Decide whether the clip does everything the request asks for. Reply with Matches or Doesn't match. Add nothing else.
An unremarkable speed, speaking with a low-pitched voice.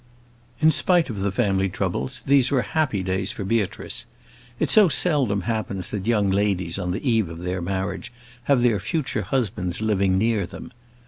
Matches